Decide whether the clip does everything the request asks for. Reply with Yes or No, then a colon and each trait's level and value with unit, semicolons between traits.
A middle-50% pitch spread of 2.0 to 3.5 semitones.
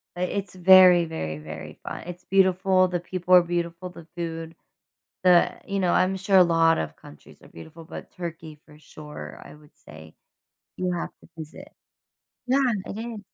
Yes: narrow, 2.5 semitones